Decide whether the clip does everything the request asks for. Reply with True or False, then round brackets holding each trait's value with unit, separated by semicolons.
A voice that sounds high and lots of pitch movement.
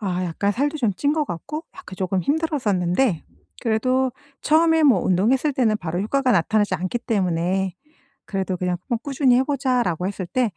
True (220 Hz; 6.4 semitones)